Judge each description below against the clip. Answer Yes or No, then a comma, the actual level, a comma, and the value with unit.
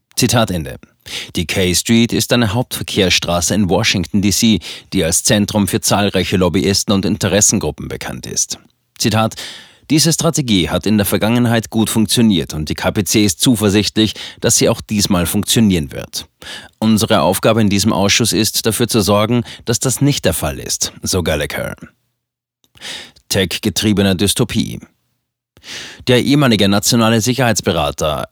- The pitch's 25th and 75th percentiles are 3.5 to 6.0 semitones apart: No, average, 2.8 semitones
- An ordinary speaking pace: Yes, average, 135 wpm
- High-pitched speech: No, low, 105 Hz